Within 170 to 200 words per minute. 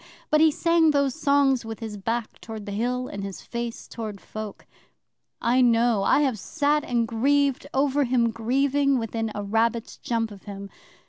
Yes: average, 175 wpm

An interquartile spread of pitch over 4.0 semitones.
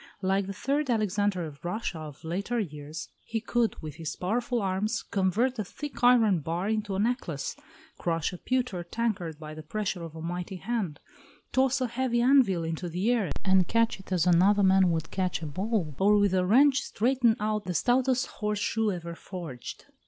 Yes: average, 5.1 semitones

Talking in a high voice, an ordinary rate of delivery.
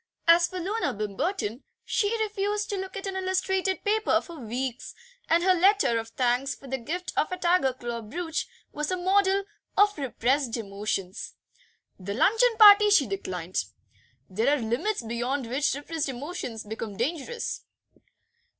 Yes: very high, 300 Hz; average, 150 wpm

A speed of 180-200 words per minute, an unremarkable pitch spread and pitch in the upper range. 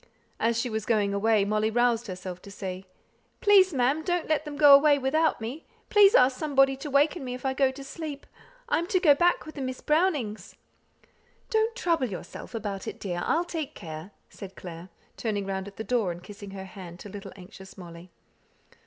No: average, 195 wpm; wide, 7.3 semitones; high, 245 Hz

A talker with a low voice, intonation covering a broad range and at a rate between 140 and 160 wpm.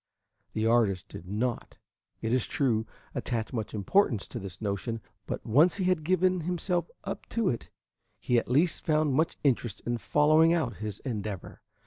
No: low, 125 Hz; wide, 6.9 semitones; average, 170 wpm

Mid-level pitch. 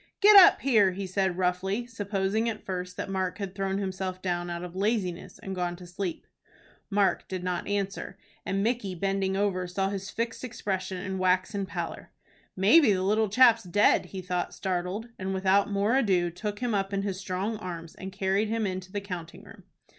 No: high, 195 Hz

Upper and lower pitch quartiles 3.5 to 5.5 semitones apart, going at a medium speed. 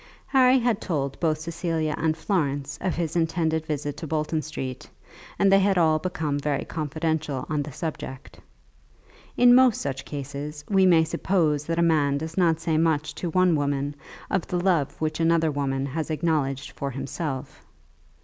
No: average, 2.8 semitones; average, 170 wpm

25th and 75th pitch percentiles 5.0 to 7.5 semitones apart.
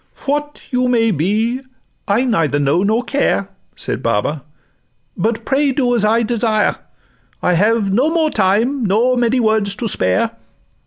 No: average, 3.9 semitones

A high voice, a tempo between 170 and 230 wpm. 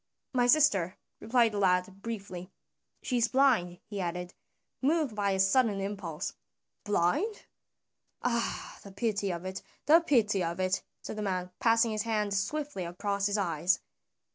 No: high, 200 Hz; average, 150 wpm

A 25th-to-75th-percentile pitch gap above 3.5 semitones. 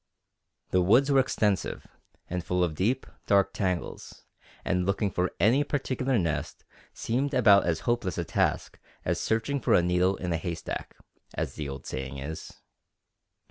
Yes: wide, 5.5 semitones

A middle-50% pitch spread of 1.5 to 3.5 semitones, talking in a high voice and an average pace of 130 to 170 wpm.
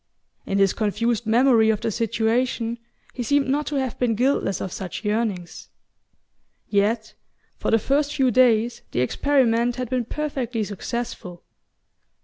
Yes: average, 3.0 semitones; high, 230 Hz; slow, 135 wpm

